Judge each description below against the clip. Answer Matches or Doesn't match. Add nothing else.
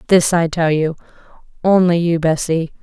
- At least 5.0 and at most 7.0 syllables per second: Doesn't match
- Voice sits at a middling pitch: Matches